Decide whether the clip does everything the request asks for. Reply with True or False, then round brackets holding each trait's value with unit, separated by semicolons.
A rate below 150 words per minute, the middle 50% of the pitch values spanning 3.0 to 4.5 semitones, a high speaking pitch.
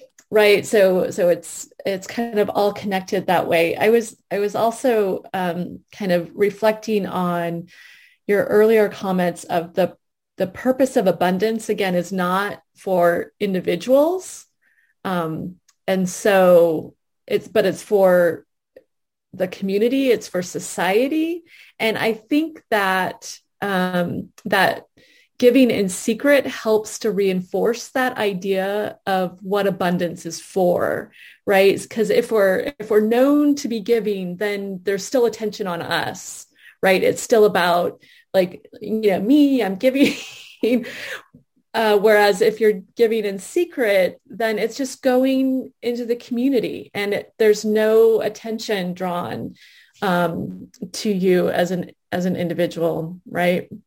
True (135 wpm; 4.0 semitones; 205 Hz)